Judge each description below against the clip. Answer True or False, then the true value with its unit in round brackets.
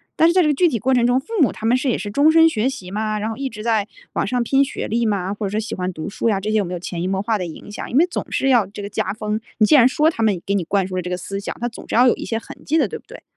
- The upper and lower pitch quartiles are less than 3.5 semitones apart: False (4.3 semitones)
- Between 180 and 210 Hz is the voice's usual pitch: False (220 Hz)